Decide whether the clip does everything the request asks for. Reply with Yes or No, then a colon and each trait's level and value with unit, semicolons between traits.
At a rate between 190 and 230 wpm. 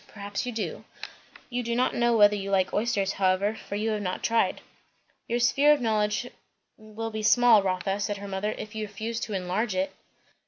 Yes: average, 195 wpm